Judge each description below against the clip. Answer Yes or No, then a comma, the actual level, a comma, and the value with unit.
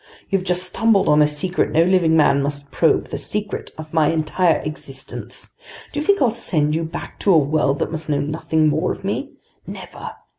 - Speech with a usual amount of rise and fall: Yes, average, 3.6 semitones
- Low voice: No, medium, 160 Hz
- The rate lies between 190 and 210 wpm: Yes, average, 200 wpm